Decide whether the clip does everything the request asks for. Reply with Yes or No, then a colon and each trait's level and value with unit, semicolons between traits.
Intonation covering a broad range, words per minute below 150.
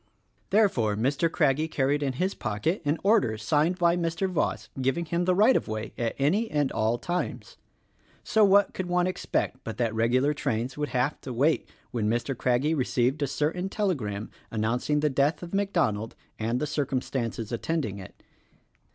No: wide, 6.4 semitones; average, 170 wpm